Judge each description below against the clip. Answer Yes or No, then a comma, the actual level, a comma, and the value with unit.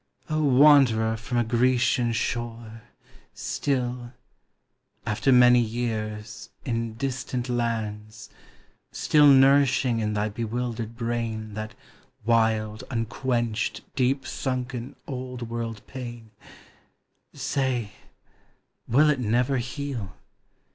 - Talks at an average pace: No, slow, 100 wpm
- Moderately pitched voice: No, low, 120 Hz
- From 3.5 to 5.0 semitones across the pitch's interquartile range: No, narrow, 2.4 semitones